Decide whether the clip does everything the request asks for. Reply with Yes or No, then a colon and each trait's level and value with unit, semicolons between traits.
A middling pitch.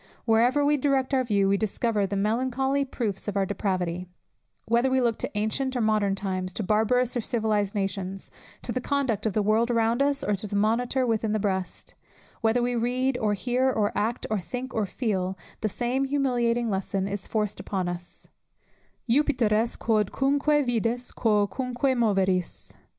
No: high, 225 Hz